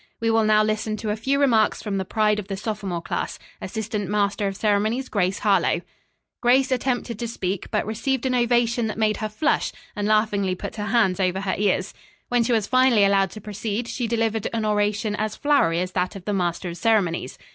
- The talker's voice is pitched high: Yes, high, 215 Hz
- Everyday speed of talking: No, fast, 210 wpm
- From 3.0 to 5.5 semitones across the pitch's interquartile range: No, narrow, 2.6 semitones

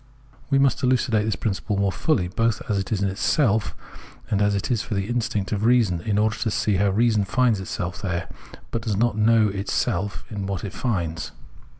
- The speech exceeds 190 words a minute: Yes, fast, 205 wpm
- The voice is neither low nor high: No, low, 105 Hz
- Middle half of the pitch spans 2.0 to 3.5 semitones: Yes, average, 2.7 semitones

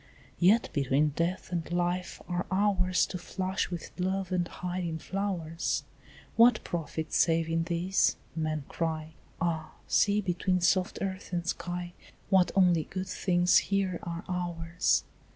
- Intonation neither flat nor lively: No, narrow, 2.0 semitones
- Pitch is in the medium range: Yes, medium, 175 Hz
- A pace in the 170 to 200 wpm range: No, average, 140 wpm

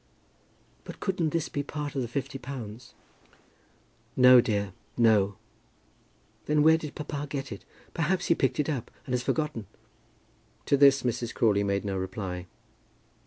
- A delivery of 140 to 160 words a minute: Yes, average, 150 wpm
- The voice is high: No, low, 130 Hz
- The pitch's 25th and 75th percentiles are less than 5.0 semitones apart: No, wide, 5.6 semitones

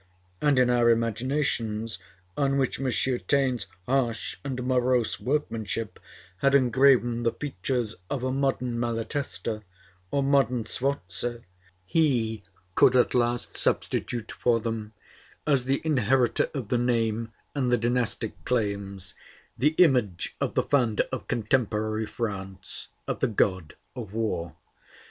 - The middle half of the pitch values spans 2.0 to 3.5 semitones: Yes, average, 3.1 semitones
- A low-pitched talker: Yes, low, 120 Hz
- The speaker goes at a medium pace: No, slow, 125 wpm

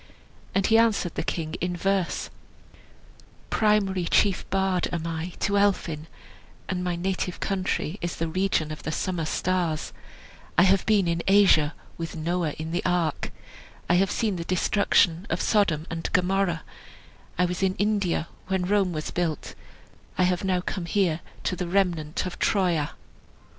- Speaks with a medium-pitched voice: Yes, medium, 180 Hz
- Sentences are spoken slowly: No, average, 160 wpm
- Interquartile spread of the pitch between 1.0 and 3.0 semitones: Yes, narrow, 2.6 semitones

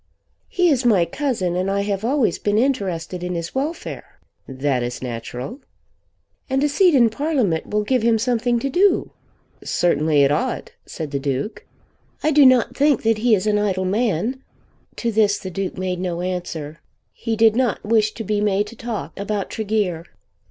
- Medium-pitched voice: No, high, 210 Hz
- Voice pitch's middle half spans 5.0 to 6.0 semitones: Yes, wide, 5.4 semitones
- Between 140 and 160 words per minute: No, average, 180 wpm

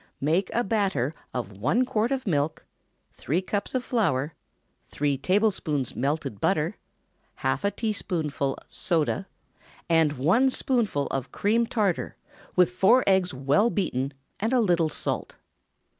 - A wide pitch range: Yes, wide, 6.8 semitones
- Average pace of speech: No, slow, 130 wpm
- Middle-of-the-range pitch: Yes, medium, 180 Hz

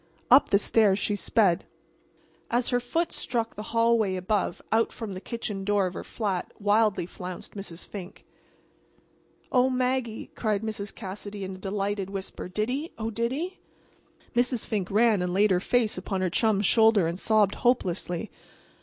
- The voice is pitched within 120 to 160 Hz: No, high, 210 Hz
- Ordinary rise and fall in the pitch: Yes, average, 3.2 semitones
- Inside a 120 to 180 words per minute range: Yes, average, 165 wpm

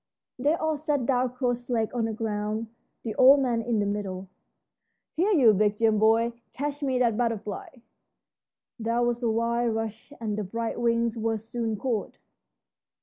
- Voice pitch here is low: No, high, 230 Hz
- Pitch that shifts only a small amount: Yes, narrow, 2.1 semitones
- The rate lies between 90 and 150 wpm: No, average, 165 wpm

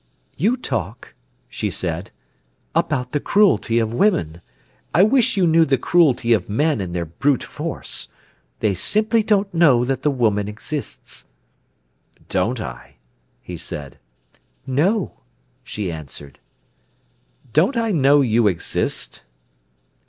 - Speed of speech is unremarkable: No, slow, 125 wpm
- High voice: No, low, 130 Hz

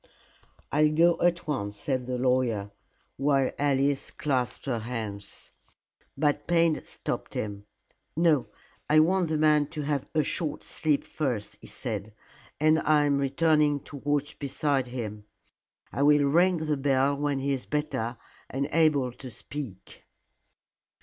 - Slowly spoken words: No, average, 145 wpm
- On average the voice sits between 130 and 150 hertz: Yes, medium, 140 Hz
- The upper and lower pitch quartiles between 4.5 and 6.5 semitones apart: No, average, 3.1 semitones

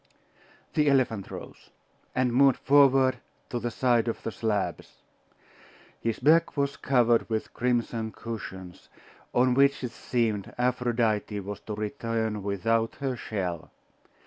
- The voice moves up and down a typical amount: Yes, average, 3.0 semitones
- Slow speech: Yes, slow, 125 wpm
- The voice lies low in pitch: Yes, low, 115 Hz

